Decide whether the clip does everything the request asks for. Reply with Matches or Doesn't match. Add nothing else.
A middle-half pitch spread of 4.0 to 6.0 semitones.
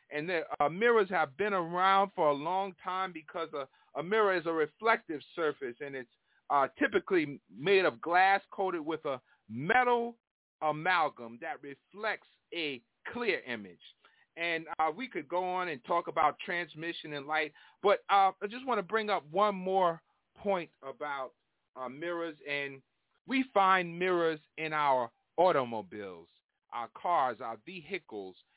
Matches